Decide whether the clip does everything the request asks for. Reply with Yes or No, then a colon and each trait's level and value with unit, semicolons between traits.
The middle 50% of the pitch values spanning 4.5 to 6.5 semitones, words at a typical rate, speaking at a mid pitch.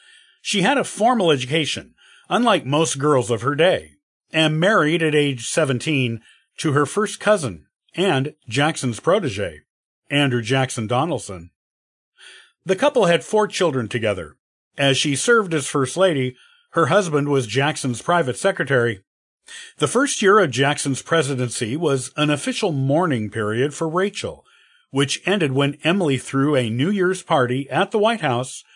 Yes: average, 4.9 semitones; average, 145 wpm; medium, 145 Hz